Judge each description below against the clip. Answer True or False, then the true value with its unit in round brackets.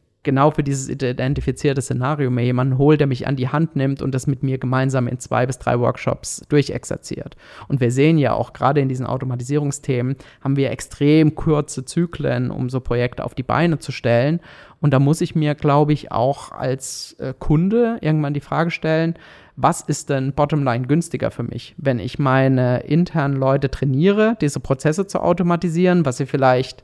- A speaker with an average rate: True (180 wpm)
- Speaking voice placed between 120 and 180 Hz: True (140 Hz)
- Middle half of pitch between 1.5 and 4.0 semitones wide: True (2.7 semitones)